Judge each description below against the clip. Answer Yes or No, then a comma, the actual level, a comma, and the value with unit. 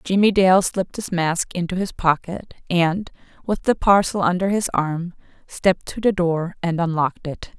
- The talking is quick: No, average, 175 wpm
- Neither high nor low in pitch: Yes, medium, 180 Hz